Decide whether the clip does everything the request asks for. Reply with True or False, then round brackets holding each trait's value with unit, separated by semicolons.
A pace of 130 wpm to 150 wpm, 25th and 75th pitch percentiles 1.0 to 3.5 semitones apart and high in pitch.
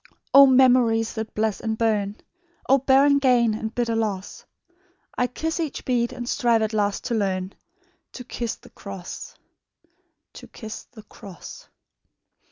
True (145 wpm; 2.9 semitones; 225 Hz)